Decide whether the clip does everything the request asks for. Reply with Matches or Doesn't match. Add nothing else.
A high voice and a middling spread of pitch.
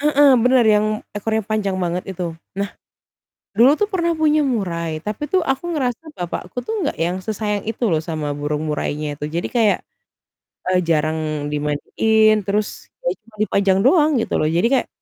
Doesn't match